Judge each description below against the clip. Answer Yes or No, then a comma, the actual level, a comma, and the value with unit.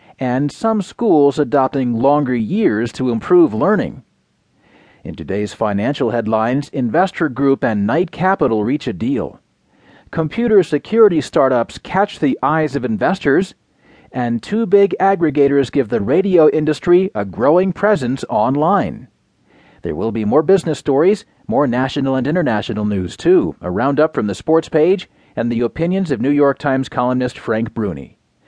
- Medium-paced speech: Yes, average, 145 wpm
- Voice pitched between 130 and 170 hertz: Yes, medium, 140 Hz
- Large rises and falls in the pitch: Yes, wide, 5.8 semitones